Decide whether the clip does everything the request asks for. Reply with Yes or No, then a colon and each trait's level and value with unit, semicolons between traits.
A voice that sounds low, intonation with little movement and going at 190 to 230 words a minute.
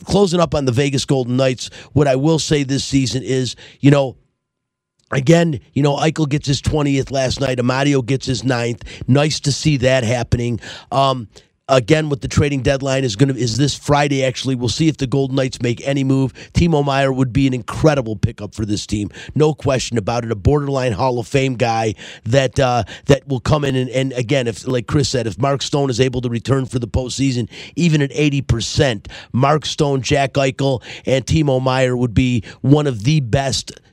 Yes: low, 130 Hz; narrow, 2.3 semitones; fast, 205 wpm